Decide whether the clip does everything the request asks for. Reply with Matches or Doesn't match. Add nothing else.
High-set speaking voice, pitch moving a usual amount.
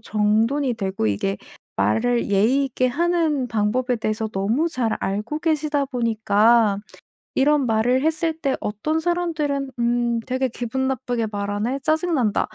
Matches